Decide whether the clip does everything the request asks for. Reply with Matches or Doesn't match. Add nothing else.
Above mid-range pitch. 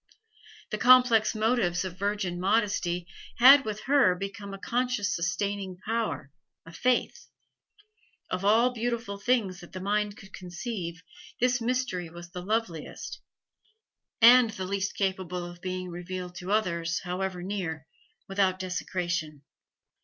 Matches